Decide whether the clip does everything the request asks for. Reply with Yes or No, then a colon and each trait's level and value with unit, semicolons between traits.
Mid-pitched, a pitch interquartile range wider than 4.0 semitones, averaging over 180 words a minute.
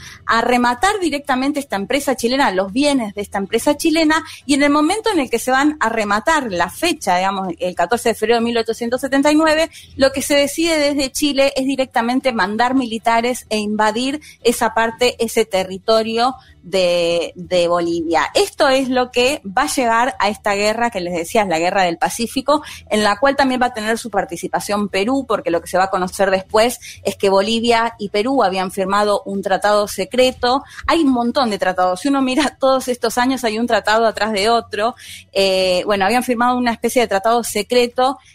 No: high, 230 Hz; average, 4.7 semitones; fast, 190 wpm